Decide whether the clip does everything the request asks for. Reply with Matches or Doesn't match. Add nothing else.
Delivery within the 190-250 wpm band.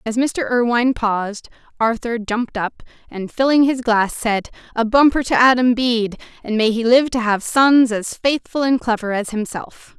Doesn't match